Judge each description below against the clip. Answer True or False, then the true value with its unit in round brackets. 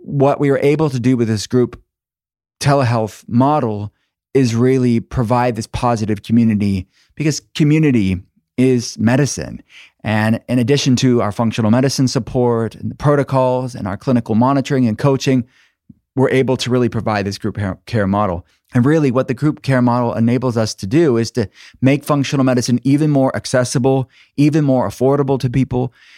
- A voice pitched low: True (125 Hz)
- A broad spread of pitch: False (3.2 semitones)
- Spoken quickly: False (165 wpm)